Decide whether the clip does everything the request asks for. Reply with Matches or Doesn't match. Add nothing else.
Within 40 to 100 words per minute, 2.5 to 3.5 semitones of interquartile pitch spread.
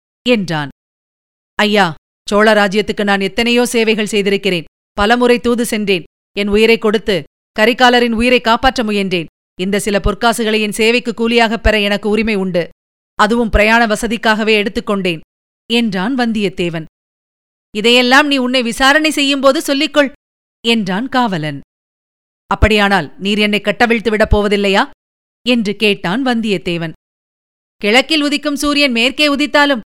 Doesn't match